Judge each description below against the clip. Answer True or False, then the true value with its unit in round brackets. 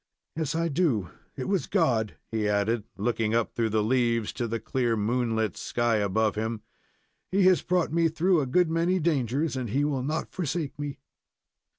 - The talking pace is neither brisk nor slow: True (180 wpm)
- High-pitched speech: False (125 Hz)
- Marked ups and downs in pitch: True (6.5 semitones)